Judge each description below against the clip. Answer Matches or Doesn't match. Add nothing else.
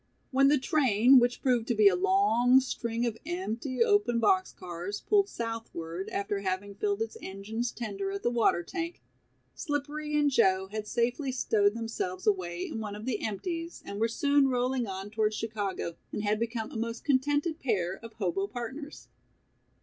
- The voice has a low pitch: Doesn't match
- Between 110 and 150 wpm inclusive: Doesn't match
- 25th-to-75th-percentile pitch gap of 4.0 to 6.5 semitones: Matches